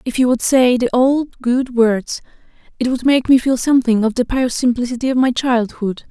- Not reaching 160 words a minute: No, fast, 205 wpm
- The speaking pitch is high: Yes, very high, 250 Hz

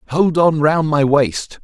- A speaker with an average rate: Yes, average, 185 wpm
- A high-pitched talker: No, medium, 150 Hz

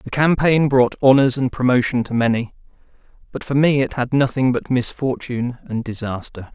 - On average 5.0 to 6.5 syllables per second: Yes, 5.2 syllables/s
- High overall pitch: No, low, 125 Hz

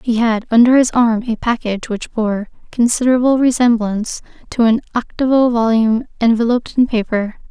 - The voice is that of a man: No, female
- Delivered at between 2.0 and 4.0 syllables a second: No, 5.5 syllables/s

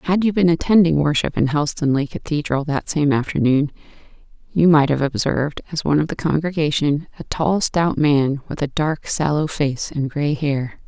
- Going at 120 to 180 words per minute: Yes, average, 175 wpm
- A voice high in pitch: No, medium, 150 Hz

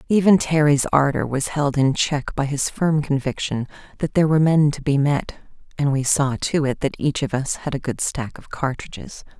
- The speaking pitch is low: No, medium, 145 Hz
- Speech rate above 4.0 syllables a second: Yes, 5.0 syllables/s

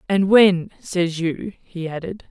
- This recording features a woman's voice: Yes, female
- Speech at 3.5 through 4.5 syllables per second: Yes, 3.6 syllables/s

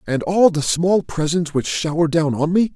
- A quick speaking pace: Yes, fast, 220 wpm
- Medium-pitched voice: Yes, medium, 165 Hz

